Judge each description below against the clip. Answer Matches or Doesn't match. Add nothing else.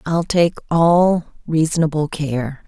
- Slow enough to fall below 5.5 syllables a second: Matches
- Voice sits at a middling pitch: Matches